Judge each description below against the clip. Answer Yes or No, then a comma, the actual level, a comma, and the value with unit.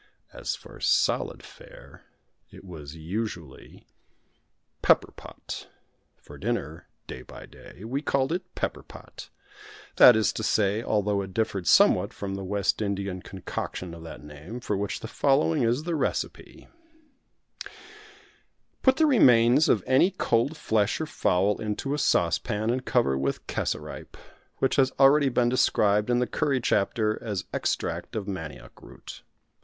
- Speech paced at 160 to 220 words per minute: No, average, 145 wpm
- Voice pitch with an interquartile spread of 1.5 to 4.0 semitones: No, average, 5.3 semitones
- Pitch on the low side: Yes, low, 110 Hz